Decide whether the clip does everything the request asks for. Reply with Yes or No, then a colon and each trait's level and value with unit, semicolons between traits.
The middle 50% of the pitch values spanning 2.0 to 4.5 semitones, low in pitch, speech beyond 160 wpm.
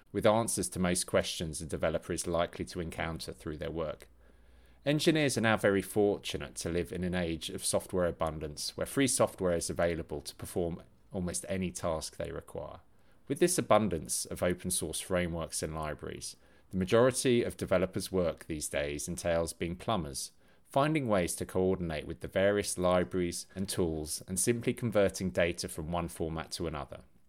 Yes: average, 3.5 semitones; very low, 90 Hz; average, 170 wpm